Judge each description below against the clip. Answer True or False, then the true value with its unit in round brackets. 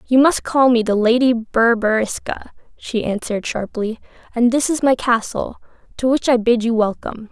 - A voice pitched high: True (235 Hz)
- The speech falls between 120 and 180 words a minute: True (170 wpm)